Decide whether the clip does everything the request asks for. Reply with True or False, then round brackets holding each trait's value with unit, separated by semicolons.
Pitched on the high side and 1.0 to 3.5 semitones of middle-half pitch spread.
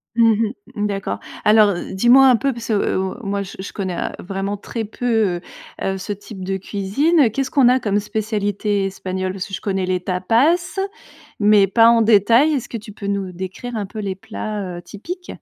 True (205 Hz; 3.0 semitones)